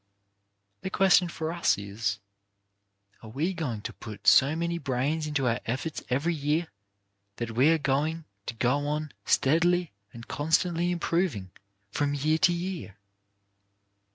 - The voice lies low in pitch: No, medium, 150 Hz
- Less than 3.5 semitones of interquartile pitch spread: No, average, 5.1 semitones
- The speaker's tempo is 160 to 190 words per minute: No, average, 140 wpm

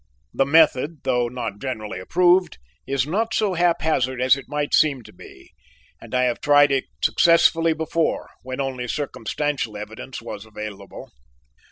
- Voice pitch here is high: No, low, 135 Hz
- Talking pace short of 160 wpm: Yes, average, 150 wpm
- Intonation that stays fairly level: No, average, 4.5 semitones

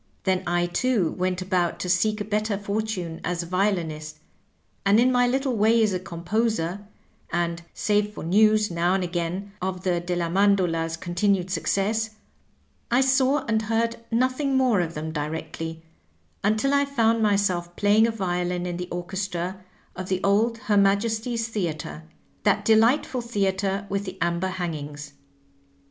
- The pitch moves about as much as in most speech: Yes, average, 3.9 semitones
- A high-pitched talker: Yes, high, 195 Hz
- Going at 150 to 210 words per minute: Yes, average, 155 wpm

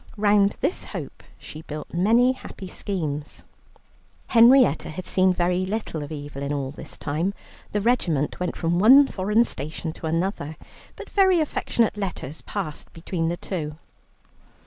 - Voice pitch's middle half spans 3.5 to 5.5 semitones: Yes, average, 5.2 semitones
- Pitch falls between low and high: Yes, medium, 180 Hz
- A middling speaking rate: Yes, average, 145 wpm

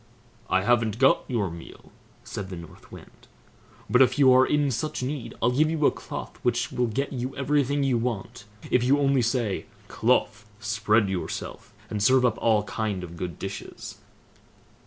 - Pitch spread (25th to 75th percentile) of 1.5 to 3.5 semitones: No, average, 4.3 semitones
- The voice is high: No, low, 120 Hz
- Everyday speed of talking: Yes, average, 175 wpm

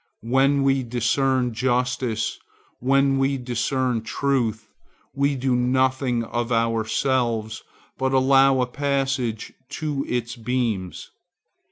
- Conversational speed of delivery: No, slow, 100 wpm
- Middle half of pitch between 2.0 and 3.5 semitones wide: Yes, narrow, 2.5 semitones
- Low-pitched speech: Yes, low, 125 Hz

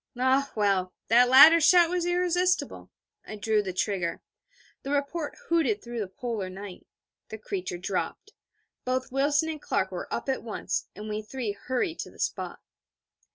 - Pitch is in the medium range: No, high, 245 Hz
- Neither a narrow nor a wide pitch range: No, wide, 6.6 semitones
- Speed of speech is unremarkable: Yes, average, 160 wpm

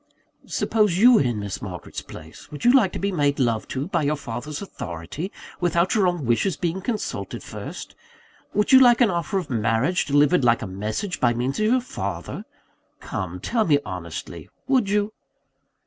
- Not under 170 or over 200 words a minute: Yes, average, 180 wpm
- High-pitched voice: No, medium, 165 Hz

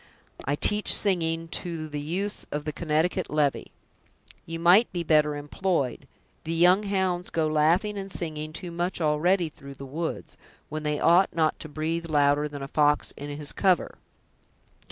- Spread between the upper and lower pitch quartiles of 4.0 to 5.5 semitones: No, average, 3.0 semitones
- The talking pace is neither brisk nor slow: Yes, average, 165 wpm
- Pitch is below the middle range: No, medium, 160 Hz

